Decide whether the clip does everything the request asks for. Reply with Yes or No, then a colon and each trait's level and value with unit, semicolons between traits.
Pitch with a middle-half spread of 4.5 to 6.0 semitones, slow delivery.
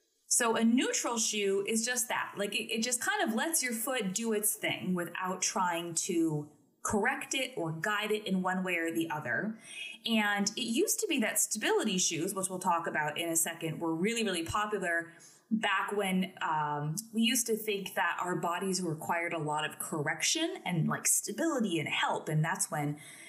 No: average, 4.9 semitones; average, 195 wpm